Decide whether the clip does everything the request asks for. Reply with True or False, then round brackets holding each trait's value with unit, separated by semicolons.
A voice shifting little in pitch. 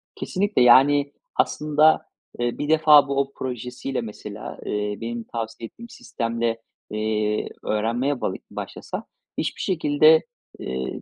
False (4.6 semitones)